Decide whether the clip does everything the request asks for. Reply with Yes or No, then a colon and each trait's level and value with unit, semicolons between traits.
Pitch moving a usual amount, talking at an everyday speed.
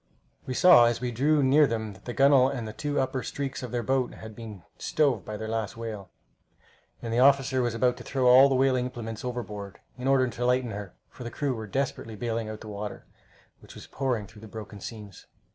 No: average, 3.1 semitones; fast, 230 wpm